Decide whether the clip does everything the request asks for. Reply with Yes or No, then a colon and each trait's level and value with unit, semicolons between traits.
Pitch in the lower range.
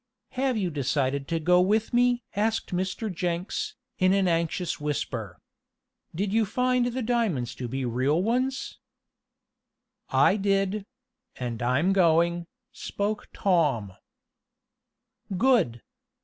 No: medium, 185 Hz